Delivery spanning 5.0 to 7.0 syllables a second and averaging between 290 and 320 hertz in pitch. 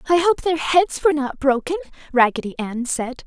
Yes: 5.3 syllables/s; very high, 295 Hz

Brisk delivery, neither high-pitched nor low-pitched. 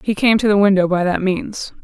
No: fast, 260 wpm; high, 200 Hz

